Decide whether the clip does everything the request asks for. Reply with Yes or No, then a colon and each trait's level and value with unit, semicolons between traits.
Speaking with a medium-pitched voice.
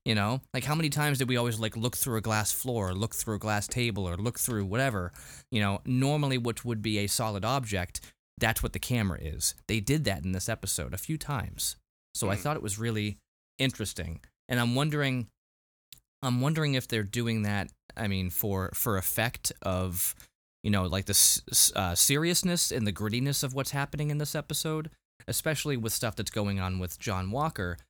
No: low, 110 Hz